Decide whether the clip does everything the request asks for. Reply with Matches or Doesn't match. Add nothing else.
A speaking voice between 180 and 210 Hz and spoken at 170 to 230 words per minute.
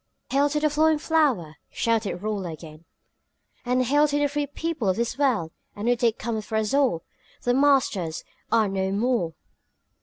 Doesn't match